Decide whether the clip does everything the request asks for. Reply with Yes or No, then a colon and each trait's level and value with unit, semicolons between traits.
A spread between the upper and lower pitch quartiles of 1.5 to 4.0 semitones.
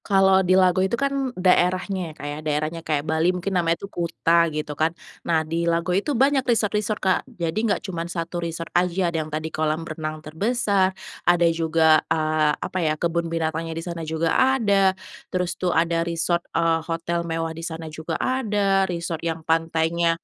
Yes: narrow, 2.6 semitones